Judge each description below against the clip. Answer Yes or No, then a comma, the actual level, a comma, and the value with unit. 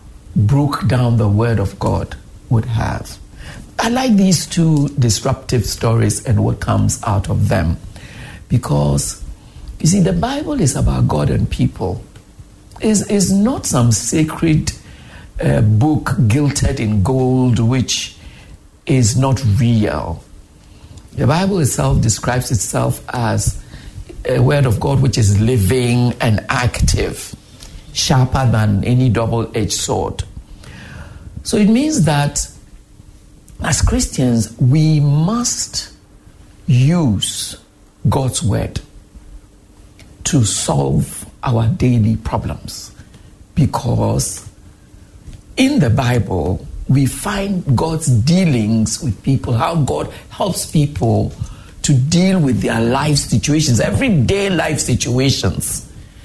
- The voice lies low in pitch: Yes, low, 120 Hz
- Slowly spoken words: Yes, slow, 110 wpm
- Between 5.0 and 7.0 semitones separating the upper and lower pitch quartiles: Yes, wide, 5.6 semitones